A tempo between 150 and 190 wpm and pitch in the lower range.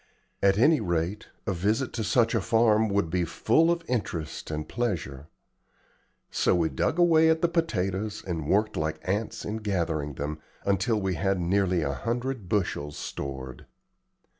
Yes: average, 160 wpm; low, 100 Hz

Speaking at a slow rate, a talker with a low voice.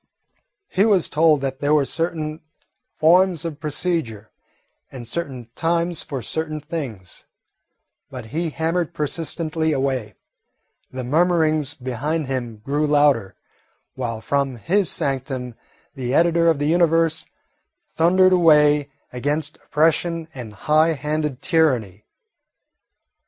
No: slow, 115 wpm; medium, 150 Hz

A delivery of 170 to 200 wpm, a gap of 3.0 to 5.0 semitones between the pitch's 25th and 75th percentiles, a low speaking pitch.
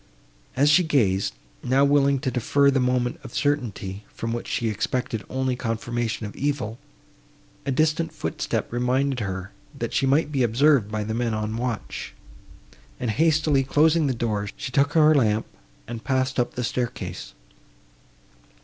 No: average, 155 wpm; average, 3.8 semitones; low, 125 Hz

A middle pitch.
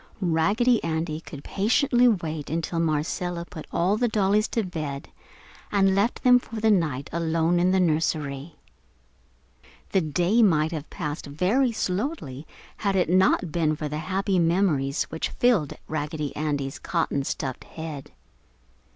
Yes: medium, 170 Hz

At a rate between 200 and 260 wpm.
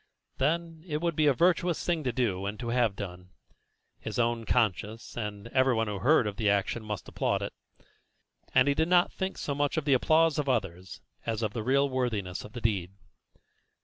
Yes: fast, 205 wpm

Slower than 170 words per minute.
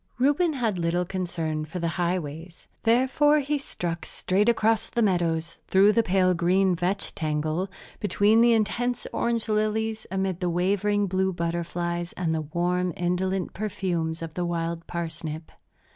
Yes: average, 145 wpm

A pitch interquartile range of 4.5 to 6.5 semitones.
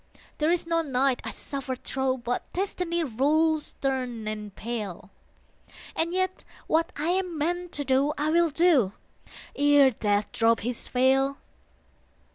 Yes: average, 5.0 semitones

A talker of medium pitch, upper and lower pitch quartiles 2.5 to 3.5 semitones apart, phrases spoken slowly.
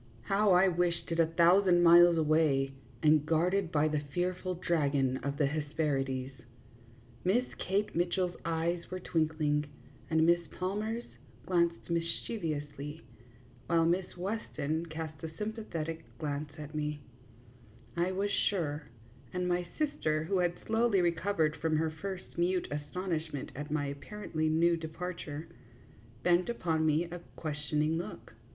Yes: medium, 165 Hz; average, 2.8 semitones; slow, 130 wpm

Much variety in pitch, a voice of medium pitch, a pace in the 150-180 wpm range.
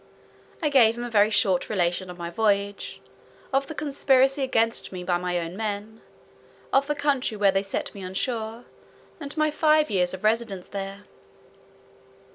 No: wide, 5.7 semitones; high, 215 Hz; average, 170 wpm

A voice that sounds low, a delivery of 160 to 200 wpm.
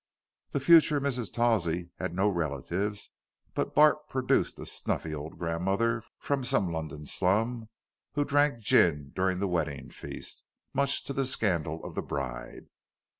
No: very low, 95 Hz; average, 145 wpm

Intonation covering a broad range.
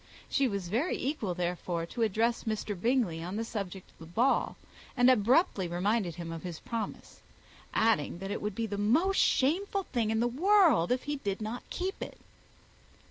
Yes: wide, 5.7 semitones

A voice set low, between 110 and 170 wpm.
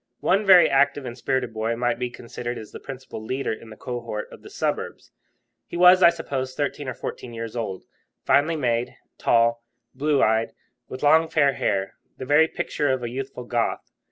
No: low, 130 Hz; average, 185 wpm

